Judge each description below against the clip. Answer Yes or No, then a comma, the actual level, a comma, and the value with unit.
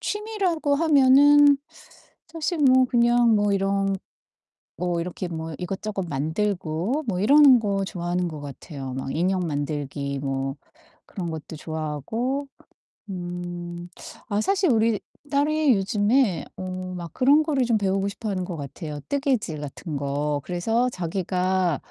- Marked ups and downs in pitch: Yes, wide, 7.8 semitones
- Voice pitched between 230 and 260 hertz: No, high, 195 Hz